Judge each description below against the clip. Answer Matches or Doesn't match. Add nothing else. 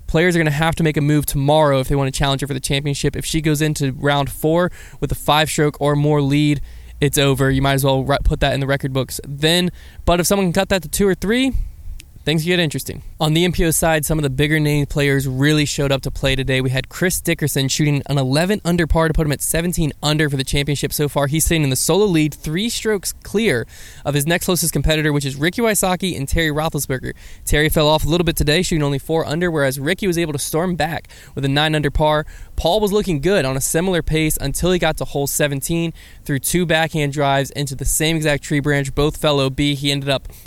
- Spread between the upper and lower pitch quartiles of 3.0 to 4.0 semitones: Doesn't match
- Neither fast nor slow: Doesn't match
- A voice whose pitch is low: Doesn't match